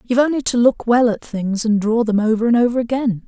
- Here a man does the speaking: No, female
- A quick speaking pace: Yes, fast, 255 wpm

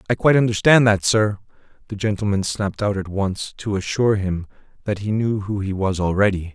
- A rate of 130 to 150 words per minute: No, average, 190 wpm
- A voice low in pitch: Yes, low, 100 Hz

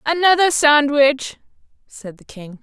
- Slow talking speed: Yes, slow, 115 wpm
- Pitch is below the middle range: No, very high, 280 Hz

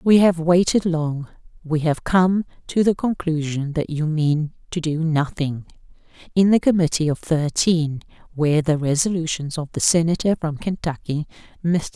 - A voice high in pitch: No, medium, 160 Hz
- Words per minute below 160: Yes, average, 150 wpm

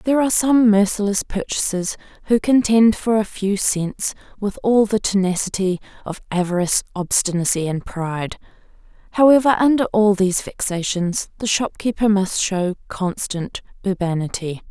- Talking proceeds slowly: Yes, slow, 125 wpm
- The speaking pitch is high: Yes, high, 200 Hz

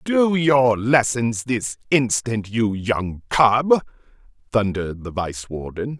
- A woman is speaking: No, male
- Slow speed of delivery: Yes, slow, 120 wpm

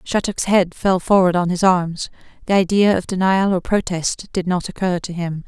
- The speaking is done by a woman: Yes, female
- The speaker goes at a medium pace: Yes, average, 185 wpm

